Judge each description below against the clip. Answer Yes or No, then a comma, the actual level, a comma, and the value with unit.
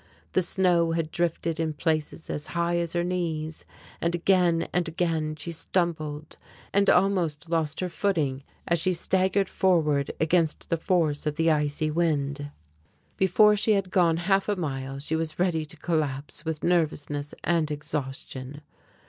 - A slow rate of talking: No, average, 155 wpm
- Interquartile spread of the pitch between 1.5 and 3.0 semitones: Yes, average, 2.7 semitones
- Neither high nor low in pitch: Yes, medium, 165 Hz